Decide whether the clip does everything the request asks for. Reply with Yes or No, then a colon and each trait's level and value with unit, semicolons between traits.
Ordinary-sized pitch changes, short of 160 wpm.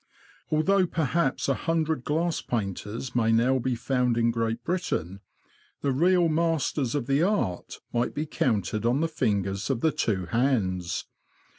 No: wide, 5.8 semitones; average, 150 wpm